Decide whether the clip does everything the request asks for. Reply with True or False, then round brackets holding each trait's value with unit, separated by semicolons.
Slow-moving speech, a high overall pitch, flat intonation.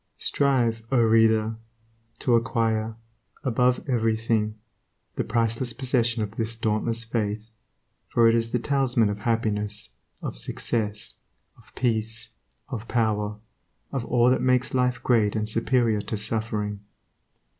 False (125 wpm; 115 Hz; 1.8 semitones)